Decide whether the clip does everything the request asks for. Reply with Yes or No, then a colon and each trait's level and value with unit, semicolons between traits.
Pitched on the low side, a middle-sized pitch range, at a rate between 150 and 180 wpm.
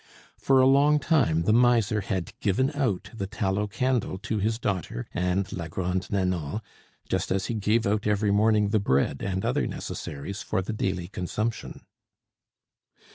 Yes: low, 100 Hz; average, 3.3 semitones; average, 160 wpm